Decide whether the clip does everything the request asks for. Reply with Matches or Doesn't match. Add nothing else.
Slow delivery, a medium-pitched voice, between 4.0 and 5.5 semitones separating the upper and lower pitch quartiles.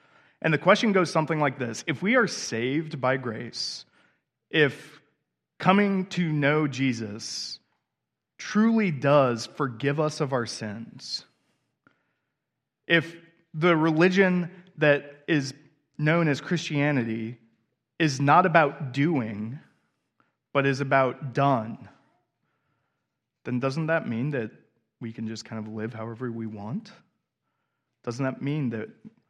Matches